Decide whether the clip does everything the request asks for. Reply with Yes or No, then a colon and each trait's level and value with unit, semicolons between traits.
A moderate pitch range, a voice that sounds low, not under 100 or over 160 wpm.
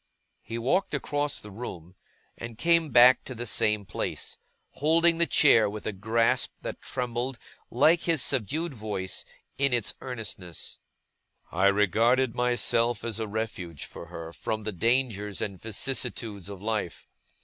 Yes: average, 4.1 semitones; low, 115 Hz; average, 145 wpm